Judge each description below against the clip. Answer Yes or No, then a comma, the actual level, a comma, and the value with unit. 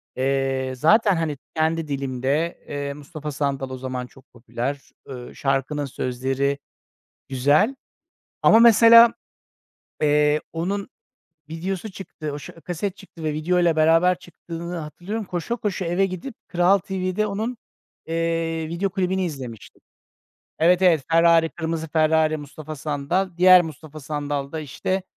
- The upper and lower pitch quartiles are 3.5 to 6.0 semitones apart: Yes, average, 4.2 semitones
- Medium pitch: Yes, medium, 160 Hz